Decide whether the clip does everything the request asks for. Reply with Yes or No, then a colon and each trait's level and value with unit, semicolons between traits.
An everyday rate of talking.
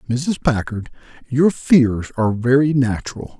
No: slow, 125 wpm